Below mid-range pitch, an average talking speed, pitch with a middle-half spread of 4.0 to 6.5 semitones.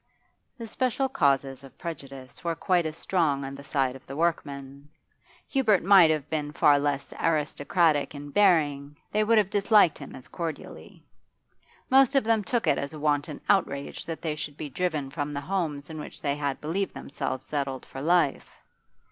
No: medium, 150 Hz; average, 180 wpm; average, 4.3 semitones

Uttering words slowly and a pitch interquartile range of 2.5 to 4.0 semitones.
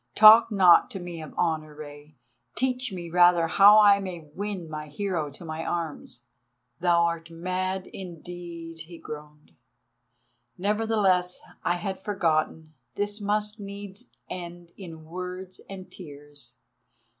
Yes: slow, 120 wpm; average, 3.5 semitones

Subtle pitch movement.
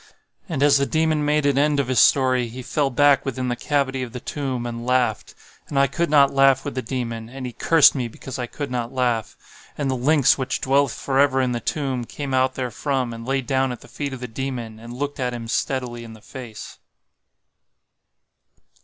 Yes: narrow, 2.3 semitones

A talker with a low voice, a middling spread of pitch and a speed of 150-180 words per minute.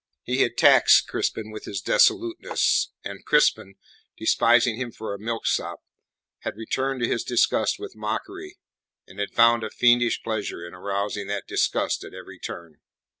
Yes: low, 115 Hz; average, 3.1 semitones; average, 155 wpm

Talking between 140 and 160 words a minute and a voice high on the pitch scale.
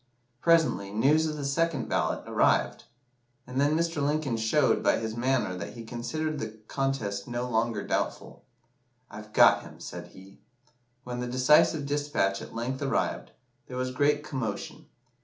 No: average, 155 wpm; low, 125 Hz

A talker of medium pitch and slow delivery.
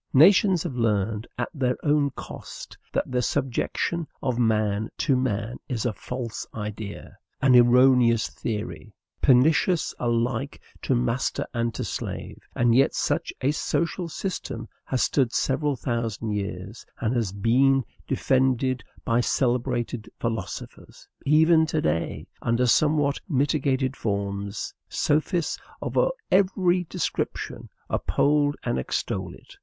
No: low, 125 Hz; slow, 125 wpm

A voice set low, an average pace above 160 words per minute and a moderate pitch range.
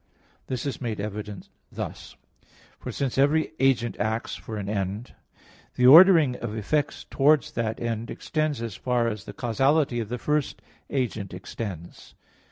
No: low, 120 Hz; average, 150 wpm; average, 4.4 semitones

